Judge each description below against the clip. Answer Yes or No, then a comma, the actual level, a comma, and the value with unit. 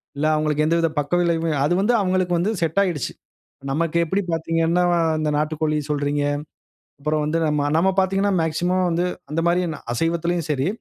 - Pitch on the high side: No, medium, 165 Hz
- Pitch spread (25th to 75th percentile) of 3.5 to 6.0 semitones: No, narrow, 2.5 semitones